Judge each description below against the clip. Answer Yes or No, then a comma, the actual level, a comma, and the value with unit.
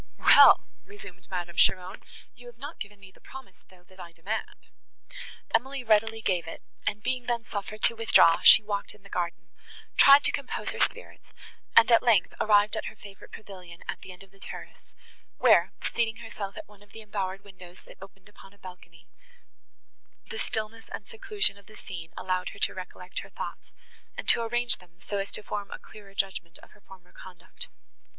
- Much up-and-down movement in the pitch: No, average, 3.3 semitones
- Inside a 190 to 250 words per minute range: Yes, average, 195 wpm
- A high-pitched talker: Yes, high, 200 Hz